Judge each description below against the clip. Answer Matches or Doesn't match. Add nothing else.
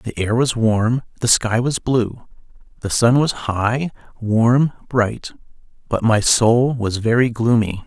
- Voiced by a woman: Doesn't match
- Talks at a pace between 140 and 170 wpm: Matches